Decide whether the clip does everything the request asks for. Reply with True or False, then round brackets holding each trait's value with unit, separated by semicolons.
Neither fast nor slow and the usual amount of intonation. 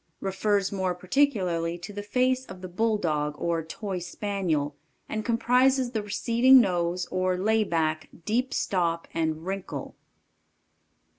False (130 wpm; 4.5 semitones)